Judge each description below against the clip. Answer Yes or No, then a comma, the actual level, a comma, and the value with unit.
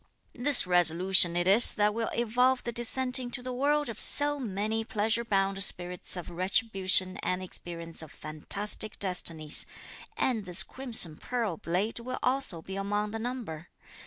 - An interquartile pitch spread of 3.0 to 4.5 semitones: No, average, 5.0 semitones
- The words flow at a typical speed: Yes, average, 160 wpm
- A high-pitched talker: Yes, high, 205 Hz